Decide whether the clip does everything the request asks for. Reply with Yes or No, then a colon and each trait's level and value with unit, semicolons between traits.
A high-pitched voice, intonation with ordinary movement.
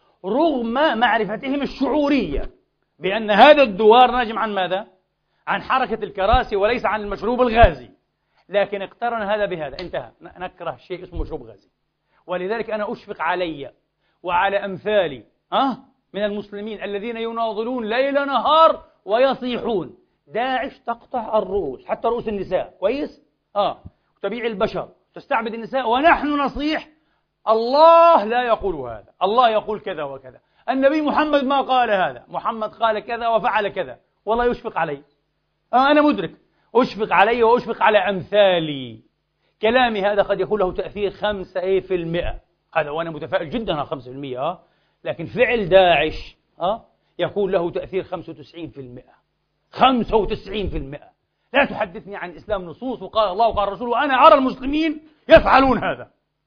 Yes: high, 220 Hz; average, 4.8 semitones